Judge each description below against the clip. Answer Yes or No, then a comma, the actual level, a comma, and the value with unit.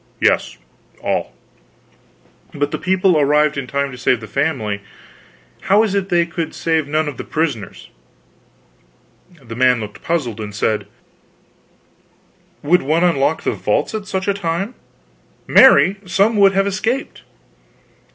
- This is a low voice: No, medium, 160 Hz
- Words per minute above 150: No, average, 140 wpm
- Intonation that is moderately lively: No, wide, 5.9 semitones